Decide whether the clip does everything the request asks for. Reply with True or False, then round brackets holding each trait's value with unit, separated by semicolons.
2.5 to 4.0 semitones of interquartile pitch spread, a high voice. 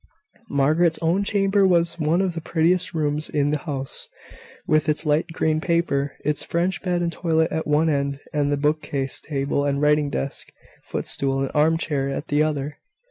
False (2.8 semitones; 155 Hz)